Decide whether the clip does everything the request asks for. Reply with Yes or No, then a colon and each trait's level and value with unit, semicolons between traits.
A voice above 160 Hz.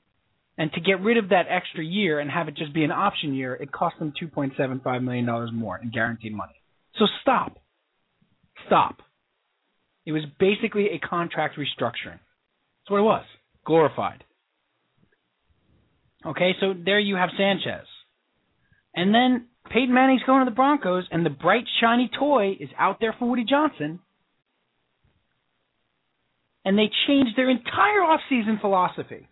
Yes: high, 190 Hz